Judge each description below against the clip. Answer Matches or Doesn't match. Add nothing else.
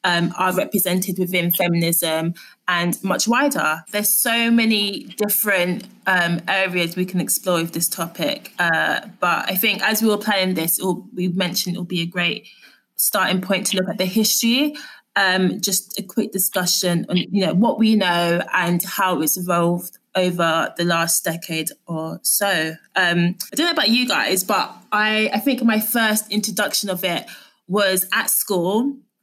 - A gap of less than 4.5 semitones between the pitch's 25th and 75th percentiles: Matches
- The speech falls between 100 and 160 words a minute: Doesn't match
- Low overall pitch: Doesn't match